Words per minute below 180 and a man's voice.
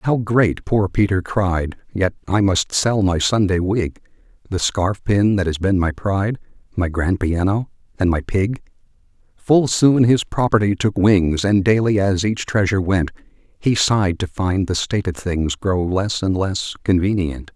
Yes: average, 170 wpm; male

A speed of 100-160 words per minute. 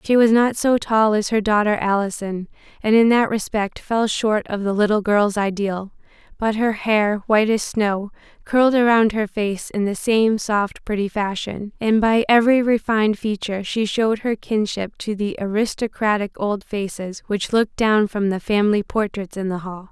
No: average, 180 wpm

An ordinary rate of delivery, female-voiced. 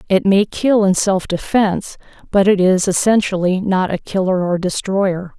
Yes: average, 165 wpm; female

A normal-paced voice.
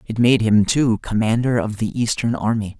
Yes: average, 195 wpm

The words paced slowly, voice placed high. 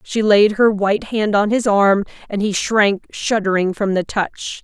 No: average, 195 wpm; high, 205 Hz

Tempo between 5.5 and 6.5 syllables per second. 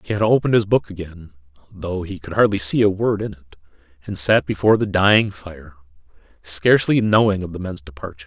Yes: 6.0 syllables/s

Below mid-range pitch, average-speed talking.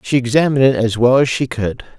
No: low, 125 Hz; fast, 240 wpm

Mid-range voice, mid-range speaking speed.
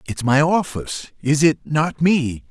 Yes: medium, 150 Hz; average, 145 wpm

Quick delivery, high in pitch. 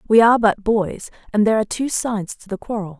Yes: fast, 240 wpm; high, 215 Hz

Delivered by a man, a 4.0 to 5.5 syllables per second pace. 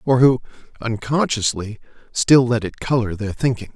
Yes: male; 4.8 syllables/s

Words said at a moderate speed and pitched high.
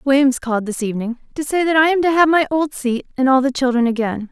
No: fast, 265 wpm; very high, 270 Hz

